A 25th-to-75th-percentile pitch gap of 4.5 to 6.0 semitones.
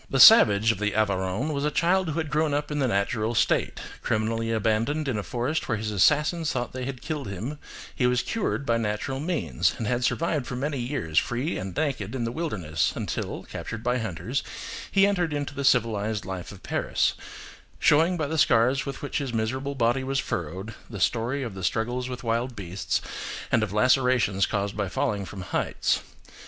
Yes: average, 4.9 semitones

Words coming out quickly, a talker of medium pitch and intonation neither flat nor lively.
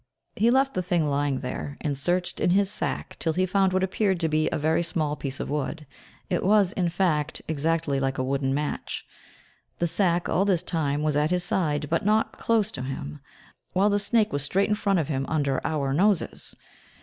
Yes: fast, 210 wpm; medium, 165 Hz; average, 4.7 semitones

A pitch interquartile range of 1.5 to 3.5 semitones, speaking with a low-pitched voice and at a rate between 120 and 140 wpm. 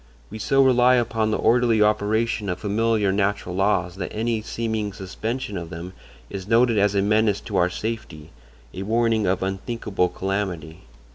No: average, 3.0 semitones; low, 105 Hz; average, 160 wpm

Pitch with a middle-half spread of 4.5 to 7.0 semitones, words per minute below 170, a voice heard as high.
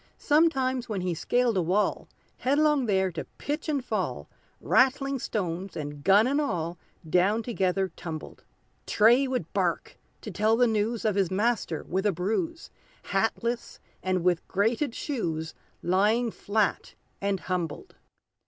Yes: average, 5.2 semitones; average, 140 wpm; high, 210 Hz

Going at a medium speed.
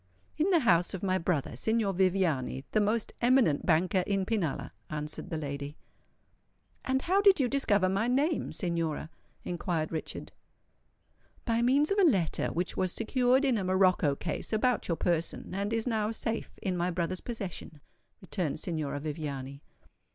Yes: average, 160 wpm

